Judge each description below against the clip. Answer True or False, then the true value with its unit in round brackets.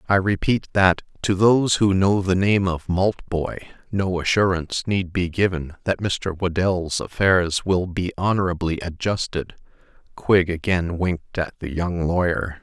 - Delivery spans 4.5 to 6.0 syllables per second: False (4.3 syllables/s)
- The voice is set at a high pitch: False (90 Hz)